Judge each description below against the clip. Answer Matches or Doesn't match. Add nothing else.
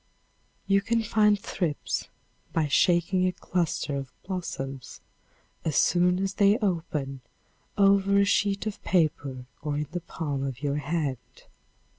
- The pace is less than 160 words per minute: Matches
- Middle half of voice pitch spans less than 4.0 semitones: Doesn't match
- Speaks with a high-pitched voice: Doesn't match